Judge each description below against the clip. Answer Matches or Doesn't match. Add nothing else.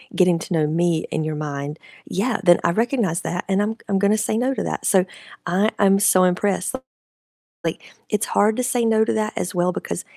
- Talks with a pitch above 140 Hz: Matches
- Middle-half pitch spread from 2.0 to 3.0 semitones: Doesn't match